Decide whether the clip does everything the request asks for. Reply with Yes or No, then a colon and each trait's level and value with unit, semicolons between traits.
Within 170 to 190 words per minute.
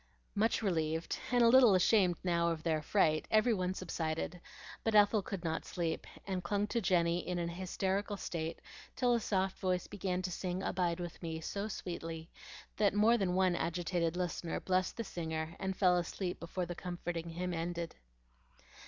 Yes: average, 175 wpm